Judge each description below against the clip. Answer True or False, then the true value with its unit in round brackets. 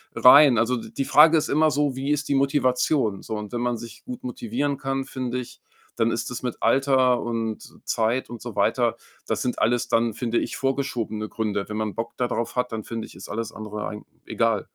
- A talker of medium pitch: False (120 Hz)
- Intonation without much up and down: False (3.2 semitones)